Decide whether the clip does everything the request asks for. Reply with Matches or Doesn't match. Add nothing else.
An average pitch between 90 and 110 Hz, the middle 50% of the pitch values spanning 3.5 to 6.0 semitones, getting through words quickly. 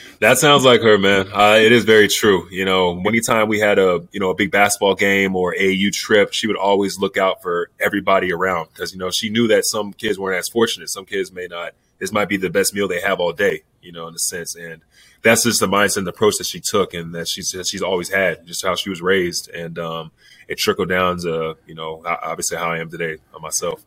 Matches